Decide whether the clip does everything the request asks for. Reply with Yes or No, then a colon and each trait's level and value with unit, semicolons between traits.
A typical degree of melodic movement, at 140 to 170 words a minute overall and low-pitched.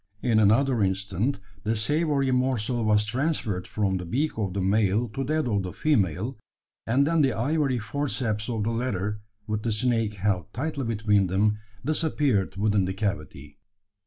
Yes: average, 4.6 semitones; average, 160 wpm; low, 110 Hz